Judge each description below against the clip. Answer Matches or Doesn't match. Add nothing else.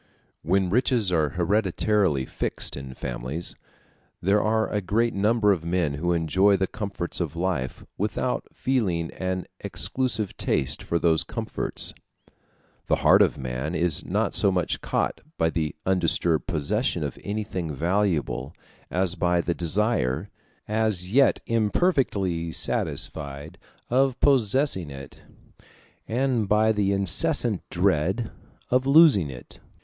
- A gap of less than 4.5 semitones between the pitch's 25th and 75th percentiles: Doesn't match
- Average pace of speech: Doesn't match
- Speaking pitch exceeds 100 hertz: Doesn't match